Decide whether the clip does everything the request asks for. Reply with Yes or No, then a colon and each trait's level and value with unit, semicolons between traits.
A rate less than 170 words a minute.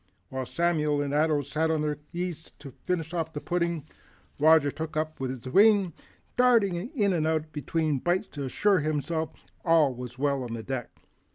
No: average, 180 wpm